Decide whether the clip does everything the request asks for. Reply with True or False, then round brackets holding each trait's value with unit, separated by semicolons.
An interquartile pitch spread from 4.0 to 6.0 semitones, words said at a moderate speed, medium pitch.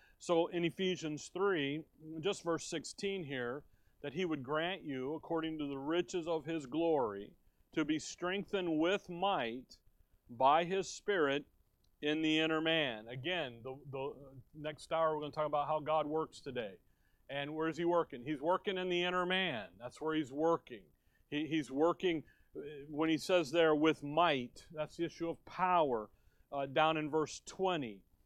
False (3.3 semitones; 170 wpm; 155 Hz)